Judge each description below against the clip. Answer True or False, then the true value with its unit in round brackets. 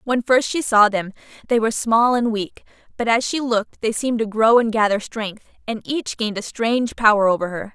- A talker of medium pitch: False (225 Hz)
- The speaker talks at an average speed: False (225 wpm)